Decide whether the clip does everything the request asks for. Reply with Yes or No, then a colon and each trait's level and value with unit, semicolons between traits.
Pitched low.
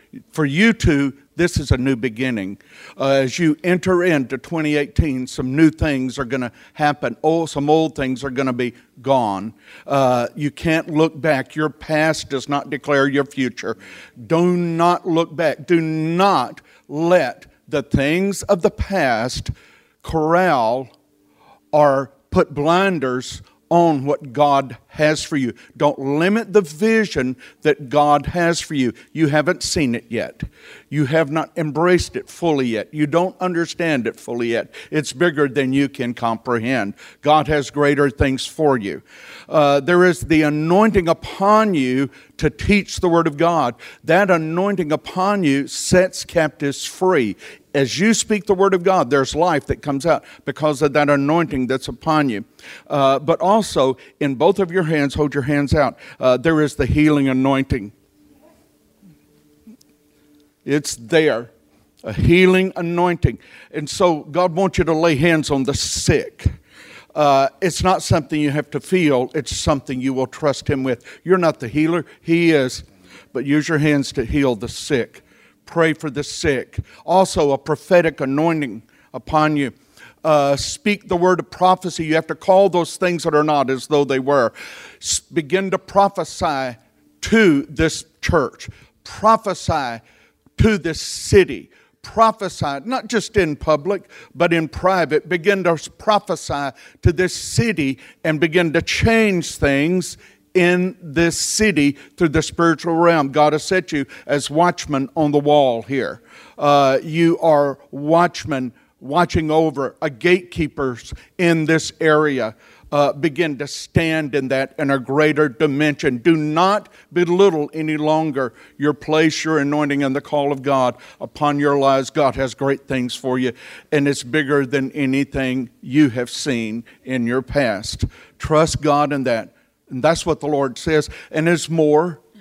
No: medium, 150 Hz